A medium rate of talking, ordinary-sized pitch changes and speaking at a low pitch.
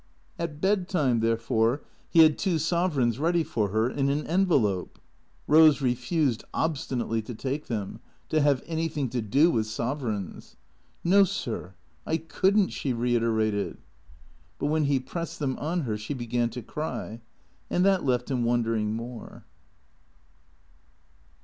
No: average, 145 wpm; wide, 5.7 semitones; low, 130 Hz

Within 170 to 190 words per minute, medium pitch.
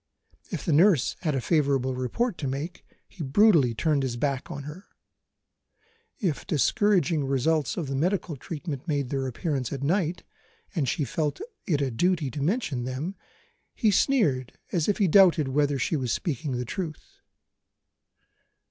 No: average, 155 wpm; medium, 150 Hz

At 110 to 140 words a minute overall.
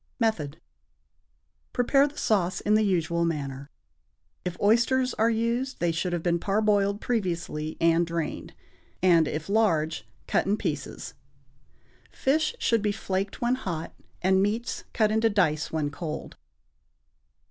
Yes: slow, 135 wpm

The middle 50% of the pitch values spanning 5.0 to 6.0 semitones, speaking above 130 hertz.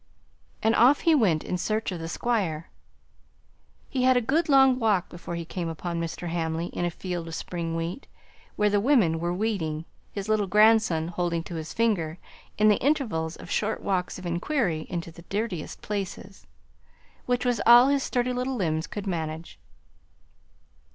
Yes: wide, 5.5 semitones; medium, 185 Hz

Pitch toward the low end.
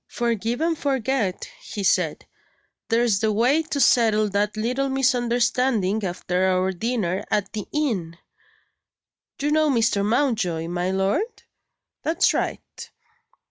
No: high, 225 Hz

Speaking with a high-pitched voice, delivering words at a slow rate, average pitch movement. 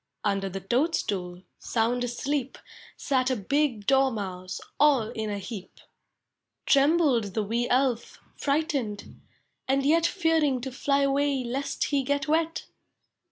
Yes: very high, 260 Hz; slow, 125 wpm; average, 4.7 semitones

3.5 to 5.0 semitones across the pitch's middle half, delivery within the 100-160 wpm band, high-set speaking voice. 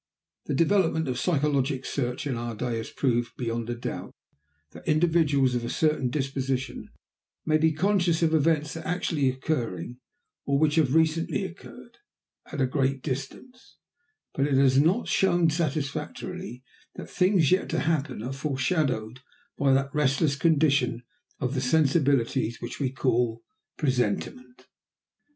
No: average, 3.9 semitones; average, 140 wpm; medium, 140 Hz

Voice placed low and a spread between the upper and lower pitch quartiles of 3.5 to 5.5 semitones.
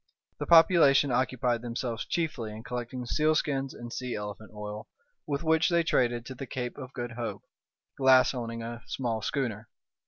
No: low, 125 Hz; average, 2.9 semitones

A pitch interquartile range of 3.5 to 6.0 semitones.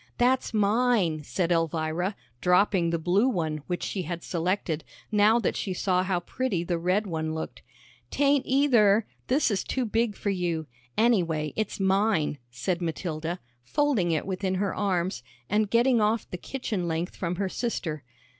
Yes: average, 4.4 semitones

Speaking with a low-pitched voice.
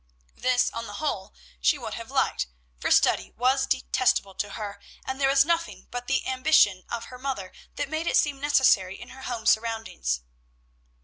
No: very high, 250 Hz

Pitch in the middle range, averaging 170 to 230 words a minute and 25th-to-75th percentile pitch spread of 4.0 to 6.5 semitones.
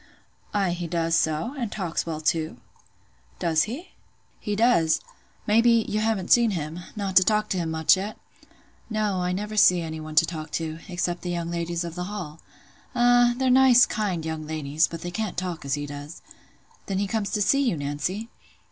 Yes: medium, 180 Hz; average, 185 wpm; average, 4.8 semitones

